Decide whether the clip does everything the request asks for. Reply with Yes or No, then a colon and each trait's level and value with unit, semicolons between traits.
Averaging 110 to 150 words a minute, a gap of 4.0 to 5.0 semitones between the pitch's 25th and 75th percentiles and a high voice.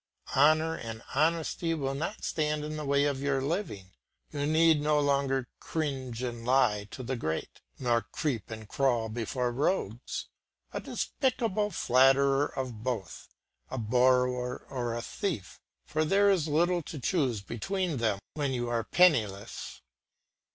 No: average, 145 wpm; average, 4.5 semitones; low, 135 Hz